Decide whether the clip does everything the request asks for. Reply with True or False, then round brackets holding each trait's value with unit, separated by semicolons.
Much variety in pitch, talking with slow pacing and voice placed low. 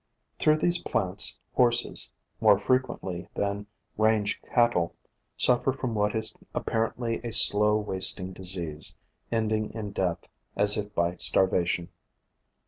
False (3.5 semitones; 120 wpm; 105 Hz)